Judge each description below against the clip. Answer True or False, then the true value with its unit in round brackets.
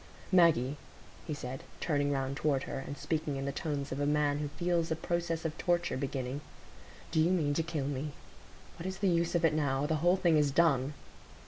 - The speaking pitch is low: False (150 Hz)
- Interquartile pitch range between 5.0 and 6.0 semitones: False (3.2 semitones)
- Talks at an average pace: False (210 wpm)